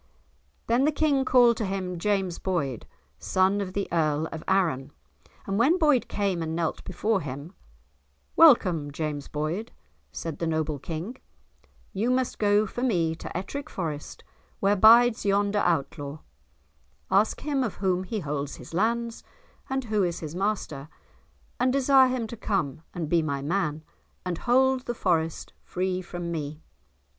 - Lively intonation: Yes, wide, 6.2 semitones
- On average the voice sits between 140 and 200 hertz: Yes, high, 190 Hz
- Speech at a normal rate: Yes, average, 155 wpm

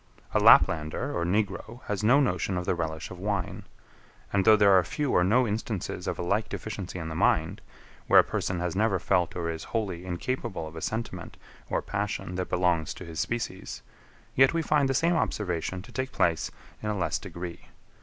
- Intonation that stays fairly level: No, average, 4.0 semitones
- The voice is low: Yes, very low, 95 Hz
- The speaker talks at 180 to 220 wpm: Yes, average, 200 wpm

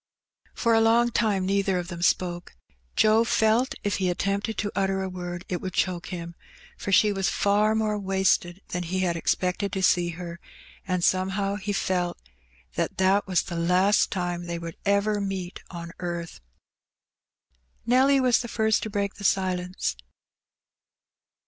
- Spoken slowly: No, average, 165 wpm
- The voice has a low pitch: No, high, 190 Hz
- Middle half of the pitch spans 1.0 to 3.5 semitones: Yes, narrow, 2.5 semitones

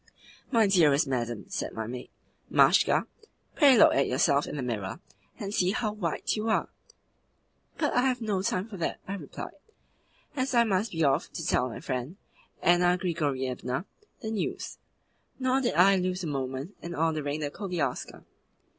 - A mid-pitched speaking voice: Yes, medium, 175 Hz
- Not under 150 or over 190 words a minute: Yes, average, 165 wpm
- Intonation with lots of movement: Yes, wide, 7.1 semitones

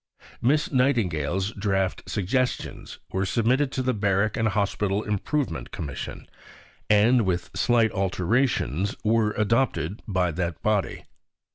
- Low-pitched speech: Yes, low, 105 Hz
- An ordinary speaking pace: No, slow, 115 wpm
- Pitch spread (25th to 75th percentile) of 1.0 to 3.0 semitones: No, average, 3.8 semitones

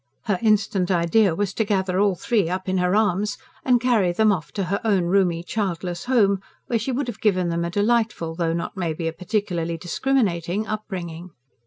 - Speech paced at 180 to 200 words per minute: Yes, average, 190 wpm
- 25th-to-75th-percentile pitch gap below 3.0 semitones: No, average, 3.7 semitones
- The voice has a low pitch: No, high, 190 Hz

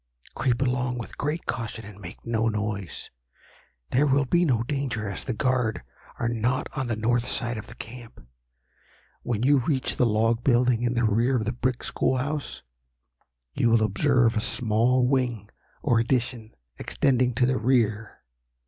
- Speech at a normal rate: Yes, average, 165 wpm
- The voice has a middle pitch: No, low, 120 Hz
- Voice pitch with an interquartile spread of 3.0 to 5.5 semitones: No, narrow, 2.4 semitones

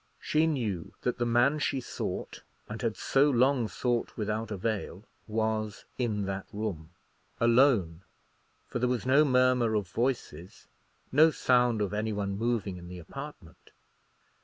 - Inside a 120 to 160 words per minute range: Yes, average, 145 wpm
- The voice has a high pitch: No, low, 115 Hz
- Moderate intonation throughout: Yes, average, 3.8 semitones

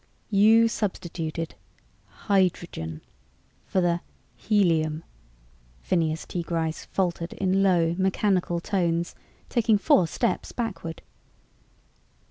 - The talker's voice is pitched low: No, medium, 175 Hz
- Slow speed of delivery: Yes, slow, 90 wpm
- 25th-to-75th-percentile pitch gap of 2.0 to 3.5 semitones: Yes, average, 3.1 semitones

